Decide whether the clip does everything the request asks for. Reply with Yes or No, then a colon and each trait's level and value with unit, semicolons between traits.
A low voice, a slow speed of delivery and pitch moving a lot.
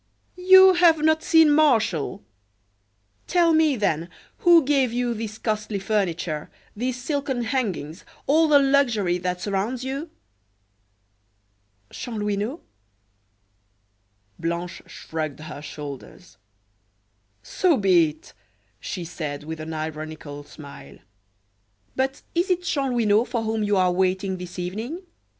No: high, 215 Hz; slow, 115 wpm; wide, 8.3 semitones